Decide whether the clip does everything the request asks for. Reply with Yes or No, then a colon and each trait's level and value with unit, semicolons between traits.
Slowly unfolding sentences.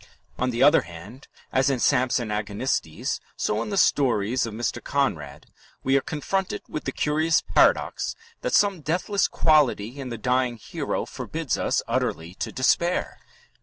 No: average, 155 wpm